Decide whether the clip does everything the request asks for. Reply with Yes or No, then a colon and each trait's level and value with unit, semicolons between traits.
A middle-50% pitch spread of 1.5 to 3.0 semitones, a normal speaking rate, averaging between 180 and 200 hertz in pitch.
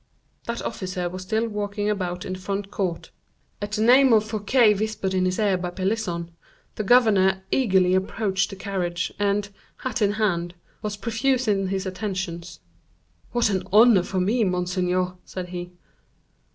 Yes: average, 2.7 semitones; average, 160 wpm; high, 195 Hz